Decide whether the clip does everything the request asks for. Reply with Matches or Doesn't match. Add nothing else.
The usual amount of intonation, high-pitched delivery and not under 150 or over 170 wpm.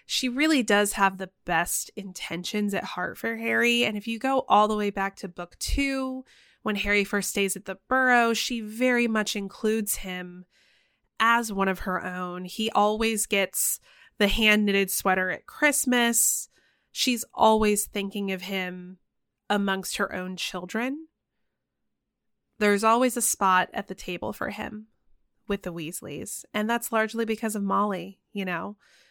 Matches